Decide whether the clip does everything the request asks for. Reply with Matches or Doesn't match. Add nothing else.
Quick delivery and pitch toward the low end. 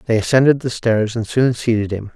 Matches